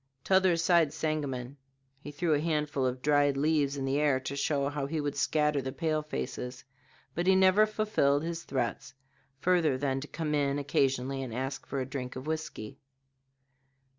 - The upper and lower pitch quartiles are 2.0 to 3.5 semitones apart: Yes, average, 2.8 semitones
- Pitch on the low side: No, medium, 145 Hz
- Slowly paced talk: No, average, 175 wpm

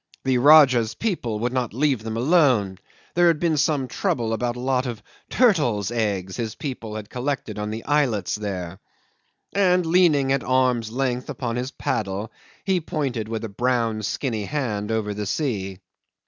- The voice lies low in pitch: Yes, low, 120 Hz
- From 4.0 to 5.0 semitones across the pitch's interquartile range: Yes, average, 4.7 semitones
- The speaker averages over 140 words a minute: Yes, average, 165 wpm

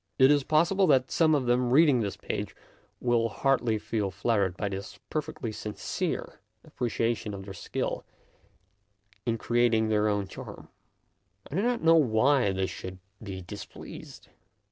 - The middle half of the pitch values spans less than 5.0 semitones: No, wide, 5.6 semitones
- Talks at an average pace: Yes, average, 155 wpm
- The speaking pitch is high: No, low, 120 Hz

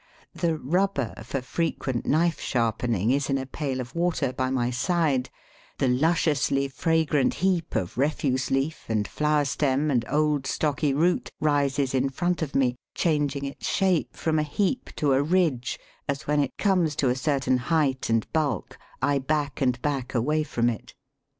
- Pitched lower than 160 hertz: Yes, medium, 140 Hz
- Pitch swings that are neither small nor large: Yes, average, 3.2 semitones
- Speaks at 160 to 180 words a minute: Yes, average, 170 wpm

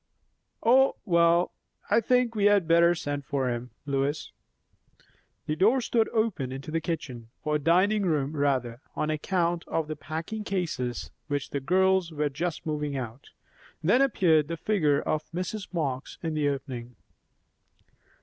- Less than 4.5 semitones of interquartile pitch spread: No, average, 4.8 semitones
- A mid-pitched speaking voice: Yes, medium, 160 Hz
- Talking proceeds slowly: No, average, 150 wpm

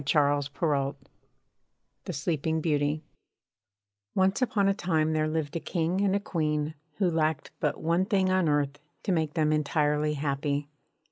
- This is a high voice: No, medium, 155 Hz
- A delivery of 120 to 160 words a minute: Yes, average, 155 wpm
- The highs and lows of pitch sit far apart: No, average, 2.9 semitones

